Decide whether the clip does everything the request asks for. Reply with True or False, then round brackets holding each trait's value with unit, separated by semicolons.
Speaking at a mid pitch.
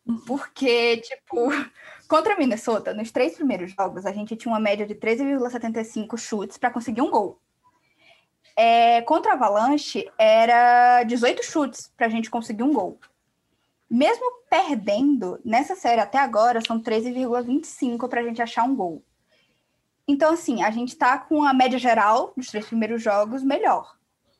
False (245 Hz)